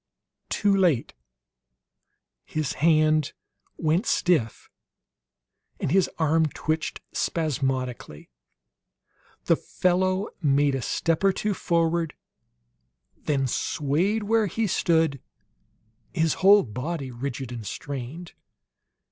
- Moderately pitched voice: Yes, medium, 160 Hz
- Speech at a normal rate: No, slow, 95 wpm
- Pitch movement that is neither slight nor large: Yes, average, 4.6 semitones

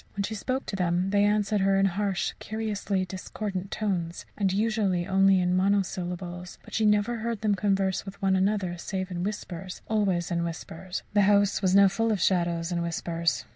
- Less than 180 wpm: No, average, 185 wpm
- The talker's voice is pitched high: Yes, high, 195 Hz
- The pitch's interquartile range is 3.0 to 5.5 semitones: No, narrow, 2.4 semitones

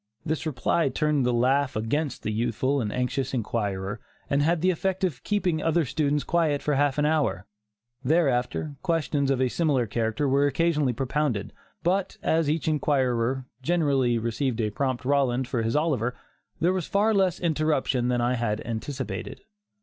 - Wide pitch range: No, average, 4.3 semitones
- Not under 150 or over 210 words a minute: Yes, average, 165 wpm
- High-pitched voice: No, medium, 140 Hz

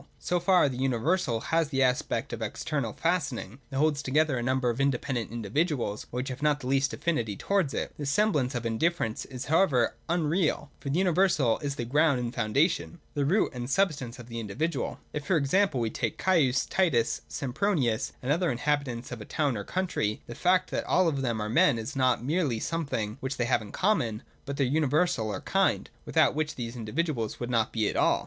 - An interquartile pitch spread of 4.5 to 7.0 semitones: Yes, average, 5.0 semitones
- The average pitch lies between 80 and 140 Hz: Yes, low, 135 Hz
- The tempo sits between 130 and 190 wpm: No, fast, 205 wpm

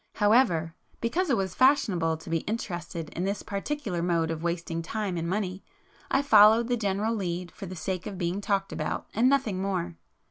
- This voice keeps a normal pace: Yes, average, 185 wpm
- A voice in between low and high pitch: No, high, 195 Hz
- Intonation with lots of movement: No, average, 4.2 semitones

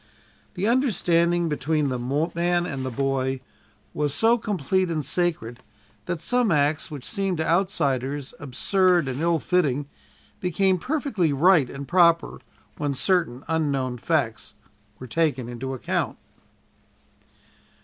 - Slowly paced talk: Yes, slow, 125 wpm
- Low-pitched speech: No, medium, 160 Hz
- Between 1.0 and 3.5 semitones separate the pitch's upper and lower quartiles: No, average, 4.9 semitones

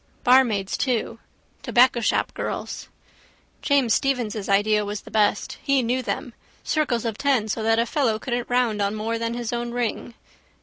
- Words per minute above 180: No, average, 150 wpm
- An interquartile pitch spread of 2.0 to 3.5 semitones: Yes, narrow, 2.5 semitones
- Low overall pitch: No, high, 235 Hz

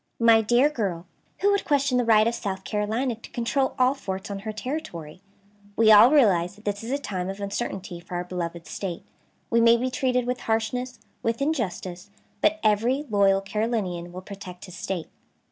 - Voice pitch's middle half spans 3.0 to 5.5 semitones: Yes, average, 4.7 semitones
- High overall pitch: Yes, high, 215 Hz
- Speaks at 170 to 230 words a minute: Yes, average, 185 wpm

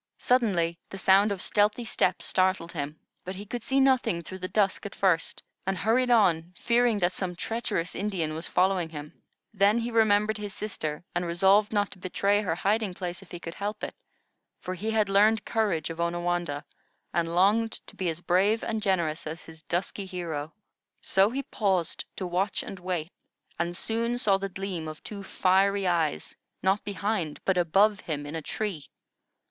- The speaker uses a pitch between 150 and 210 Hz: Yes, high, 190 Hz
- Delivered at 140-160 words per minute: No, average, 185 wpm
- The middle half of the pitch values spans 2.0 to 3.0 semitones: No, average, 3.5 semitones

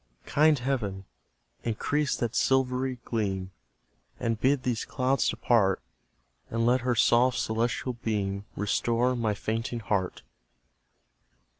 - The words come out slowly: Yes, slow, 110 wpm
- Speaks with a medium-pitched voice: No, low, 120 Hz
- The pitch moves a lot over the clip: No, average, 3.0 semitones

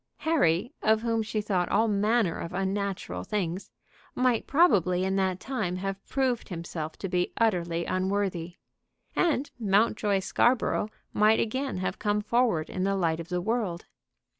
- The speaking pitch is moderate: No, high, 195 Hz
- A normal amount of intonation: Yes, average, 4.0 semitones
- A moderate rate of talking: Yes, average, 150 wpm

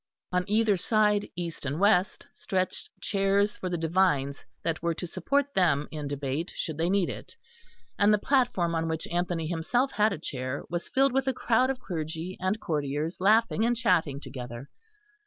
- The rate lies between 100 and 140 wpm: No, average, 175 wpm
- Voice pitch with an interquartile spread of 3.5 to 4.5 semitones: No, average, 4.9 semitones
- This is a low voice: No, medium, 180 Hz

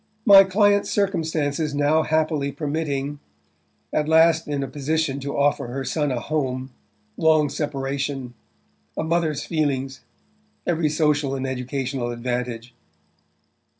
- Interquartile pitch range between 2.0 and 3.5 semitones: Yes, average, 3.0 semitones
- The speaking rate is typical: No, slow, 105 wpm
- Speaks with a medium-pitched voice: Yes, medium, 145 Hz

